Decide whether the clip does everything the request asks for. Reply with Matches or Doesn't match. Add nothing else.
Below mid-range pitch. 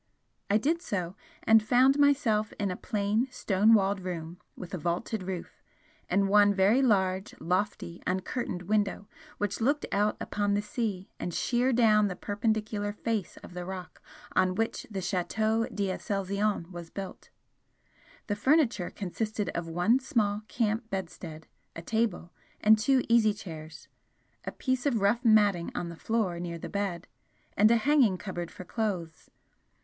Doesn't match